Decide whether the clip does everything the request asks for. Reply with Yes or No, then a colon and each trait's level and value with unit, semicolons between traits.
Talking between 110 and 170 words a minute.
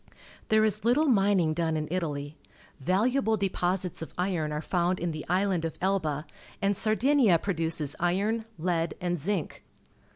Yes: average, 150 wpm